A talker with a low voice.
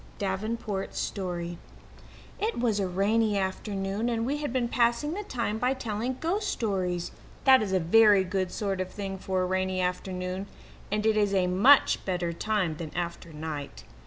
No: high, 195 Hz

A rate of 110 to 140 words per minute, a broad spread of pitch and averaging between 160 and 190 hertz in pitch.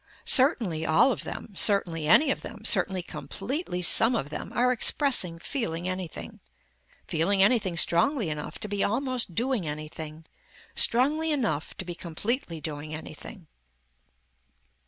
Yes: slow, 135 wpm; wide, 7.4 semitones; medium, 185 Hz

